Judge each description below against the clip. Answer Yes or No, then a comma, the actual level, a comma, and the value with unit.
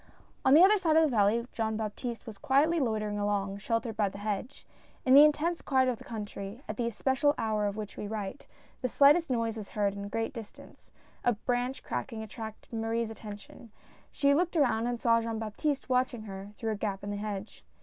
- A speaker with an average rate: No, fast, 210 wpm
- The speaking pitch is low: No, high, 225 Hz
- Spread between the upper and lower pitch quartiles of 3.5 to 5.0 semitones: Yes, average, 3.8 semitones